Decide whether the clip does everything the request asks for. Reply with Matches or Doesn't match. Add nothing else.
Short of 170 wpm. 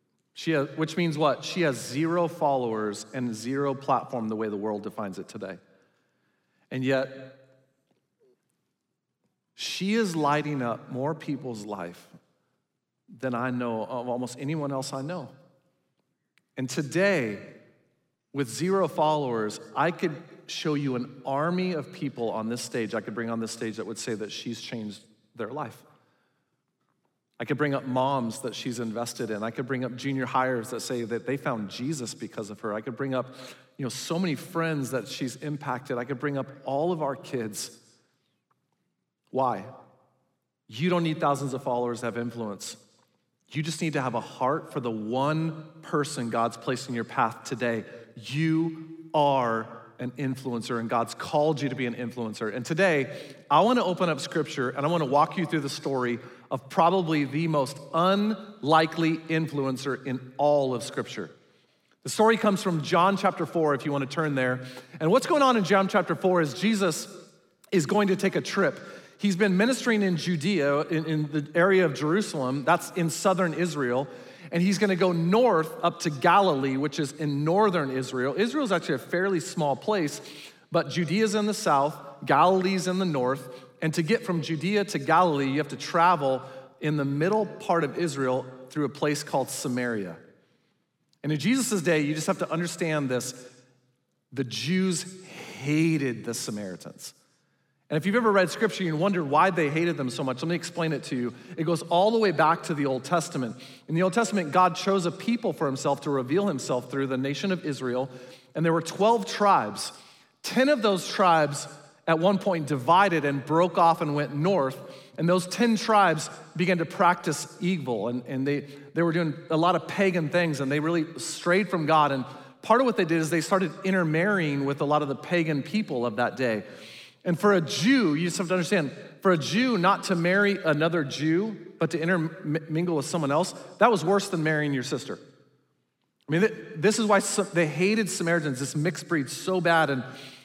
Doesn't match